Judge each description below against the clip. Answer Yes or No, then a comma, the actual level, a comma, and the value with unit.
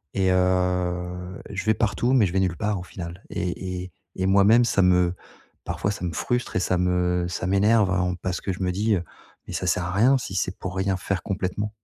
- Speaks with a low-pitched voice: Yes, very low, 95 Hz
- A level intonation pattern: Yes, narrow, 1.8 semitones